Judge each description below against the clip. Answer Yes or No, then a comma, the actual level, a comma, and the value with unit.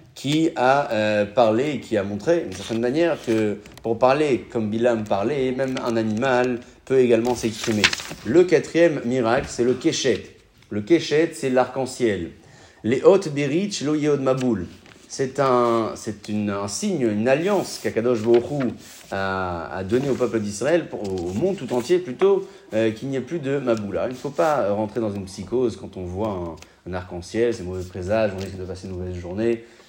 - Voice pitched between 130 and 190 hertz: No, low, 115 Hz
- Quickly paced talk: No, average, 185 wpm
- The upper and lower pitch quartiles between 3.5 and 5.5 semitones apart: Yes, average, 4.5 semitones